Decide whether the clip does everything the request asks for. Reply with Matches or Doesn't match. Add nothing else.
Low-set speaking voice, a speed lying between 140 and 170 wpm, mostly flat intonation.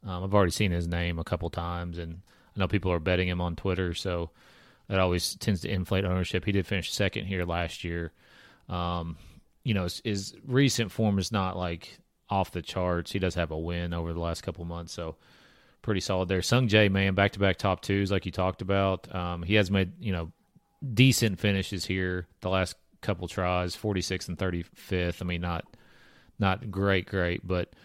Doesn't match